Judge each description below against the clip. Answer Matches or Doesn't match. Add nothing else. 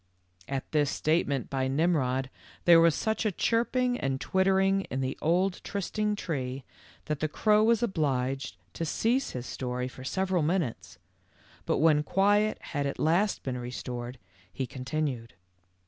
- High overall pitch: Doesn't match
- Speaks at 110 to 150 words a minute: Matches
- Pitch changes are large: Matches